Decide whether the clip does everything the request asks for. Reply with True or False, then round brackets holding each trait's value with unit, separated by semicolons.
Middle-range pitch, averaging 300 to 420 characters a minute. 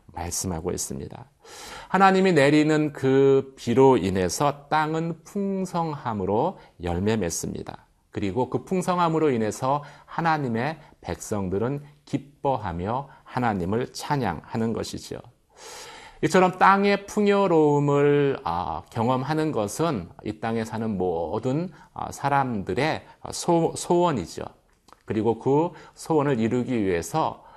False (145 Hz; 245 characters per minute)